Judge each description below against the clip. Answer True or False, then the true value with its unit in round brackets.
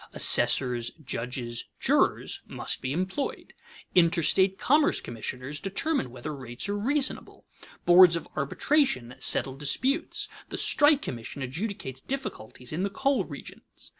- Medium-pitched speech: True (170 Hz)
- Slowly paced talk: True (120 wpm)